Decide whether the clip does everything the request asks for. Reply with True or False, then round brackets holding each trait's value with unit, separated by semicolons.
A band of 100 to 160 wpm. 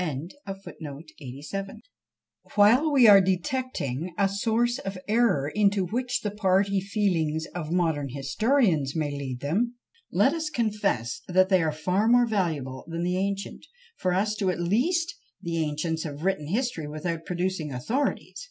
True (145 wpm)